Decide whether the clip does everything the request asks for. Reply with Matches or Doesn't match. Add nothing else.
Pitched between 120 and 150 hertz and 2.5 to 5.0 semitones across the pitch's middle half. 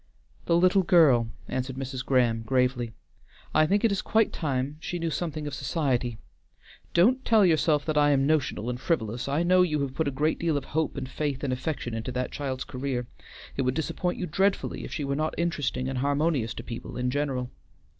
Matches